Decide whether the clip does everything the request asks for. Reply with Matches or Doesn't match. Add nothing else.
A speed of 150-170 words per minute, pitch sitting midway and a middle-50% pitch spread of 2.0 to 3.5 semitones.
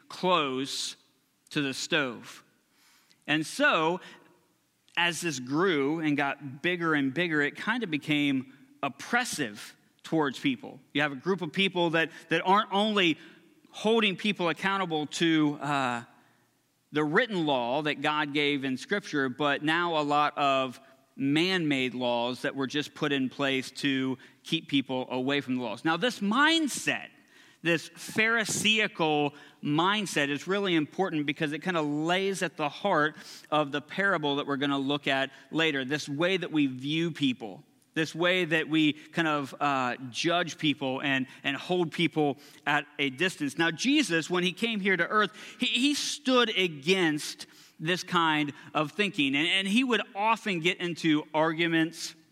Doesn't match